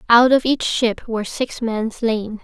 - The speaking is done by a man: No, female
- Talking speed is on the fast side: No, average, 195 wpm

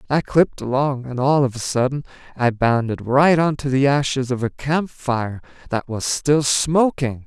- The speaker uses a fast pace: No, average, 190 wpm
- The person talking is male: Yes, male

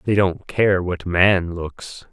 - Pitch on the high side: No, very low, 90 Hz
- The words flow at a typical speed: Yes, average, 170 wpm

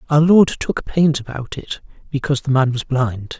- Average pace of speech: Yes, average, 195 wpm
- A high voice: No, medium, 140 Hz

